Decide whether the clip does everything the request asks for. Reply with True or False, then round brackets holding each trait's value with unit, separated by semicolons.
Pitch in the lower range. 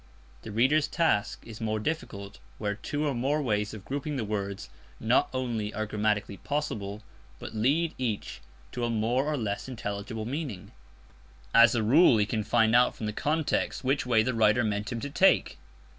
True (115 Hz)